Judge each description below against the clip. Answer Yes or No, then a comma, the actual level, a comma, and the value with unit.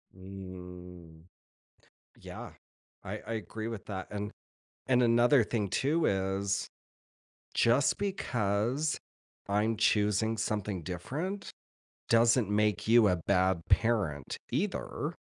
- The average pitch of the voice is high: No, low, 105 Hz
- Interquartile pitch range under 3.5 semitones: No, average, 3.8 semitones